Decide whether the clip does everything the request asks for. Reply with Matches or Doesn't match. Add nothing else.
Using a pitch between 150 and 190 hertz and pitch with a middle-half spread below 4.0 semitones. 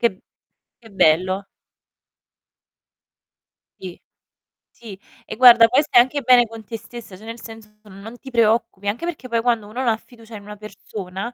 Doesn't match